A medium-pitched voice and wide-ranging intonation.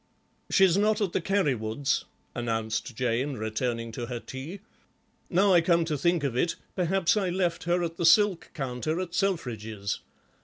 Yes: medium, 165 Hz; wide, 7.0 semitones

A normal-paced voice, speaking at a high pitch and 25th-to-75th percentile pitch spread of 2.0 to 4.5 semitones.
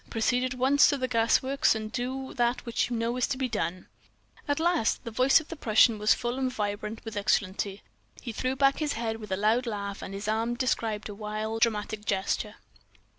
No: fast, 215 wpm; high, 230 Hz; average, 3.3 semitones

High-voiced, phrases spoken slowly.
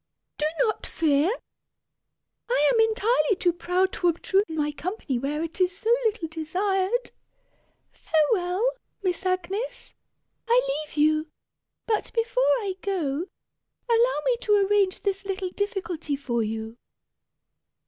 Yes: very high, 370 Hz; slow, 125 wpm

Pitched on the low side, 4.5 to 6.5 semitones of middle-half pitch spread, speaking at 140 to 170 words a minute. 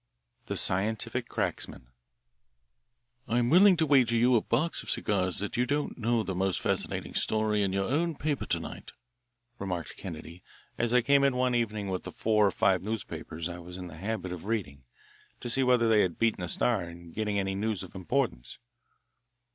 No: low, 105 Hz; average, 4.8 semitones; average, 185 wpm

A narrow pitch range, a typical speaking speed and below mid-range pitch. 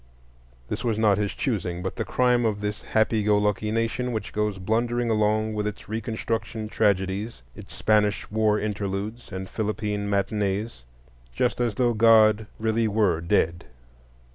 Yes: narrow, 1.6 semitones; average, 150 wpm; low, 105 Hz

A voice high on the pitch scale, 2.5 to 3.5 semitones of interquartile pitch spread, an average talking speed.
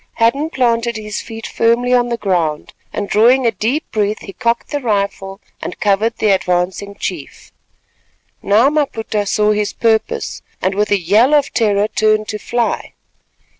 Yes: high, 215 Hz; average, 2.8 semitones; average, 160 wpm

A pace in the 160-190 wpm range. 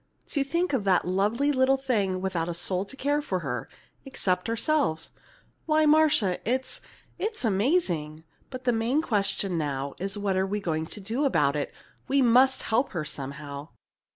Yes: average, 170 wpm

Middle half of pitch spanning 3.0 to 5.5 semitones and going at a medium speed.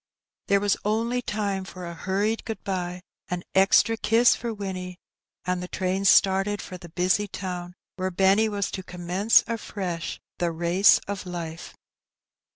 No: narrow, 2.4 semitones; average, 155 wpm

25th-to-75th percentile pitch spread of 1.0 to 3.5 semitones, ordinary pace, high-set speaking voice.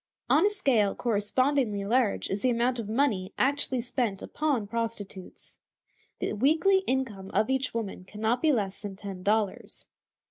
No: average, 4.6 semitones; average, 155 wpm; high, 230 Hz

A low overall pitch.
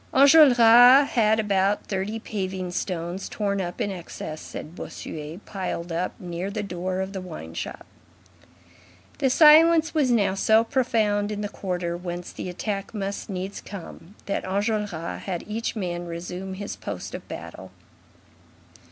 No: high, 195 Hz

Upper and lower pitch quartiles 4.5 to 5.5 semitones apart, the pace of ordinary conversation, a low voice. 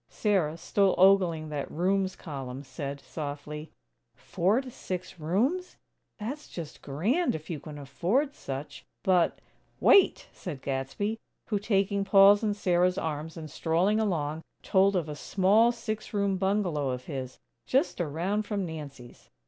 No: average, 5.2 semitones; average, 145 wpm; medium, 180 Hz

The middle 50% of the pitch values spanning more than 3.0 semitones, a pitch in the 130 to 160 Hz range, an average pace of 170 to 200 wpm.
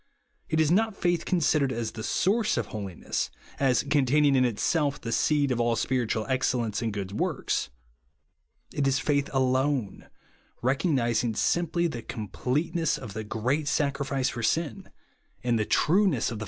Yes: average, 4.4 semitones; low, 135 Hz; average, 175 wpm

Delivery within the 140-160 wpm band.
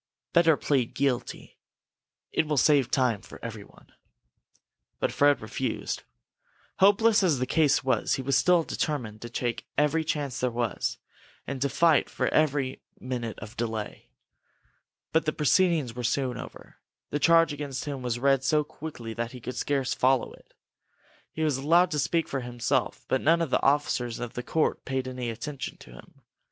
No: average, 170 wpm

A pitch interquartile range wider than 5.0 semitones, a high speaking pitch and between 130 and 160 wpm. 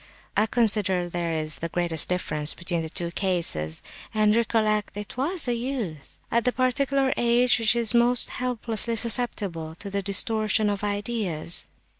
Yes: wide, 5.4 semitones; high, 210 Hz; average, 150 wpm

